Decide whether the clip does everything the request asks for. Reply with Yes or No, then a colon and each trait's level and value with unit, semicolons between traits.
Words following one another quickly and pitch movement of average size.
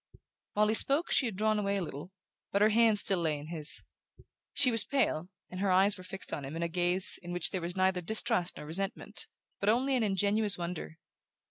Yes: fast, 220 wpm; average, 3.6 semitones